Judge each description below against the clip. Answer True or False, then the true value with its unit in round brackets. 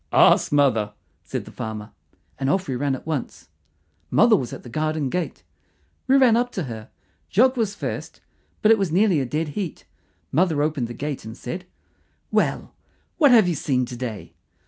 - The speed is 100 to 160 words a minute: False (185 wpm)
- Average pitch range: False (7.6 semitones)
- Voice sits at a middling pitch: True (150 Hz)